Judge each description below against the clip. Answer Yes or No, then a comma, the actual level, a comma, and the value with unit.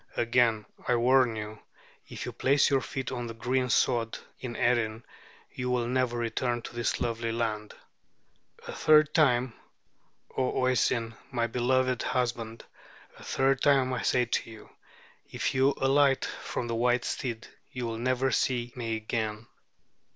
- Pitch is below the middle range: Yes, low, 120 Hz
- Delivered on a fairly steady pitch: Yes, narrow, 2.0 semitones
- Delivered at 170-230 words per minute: No, average, 150 wpm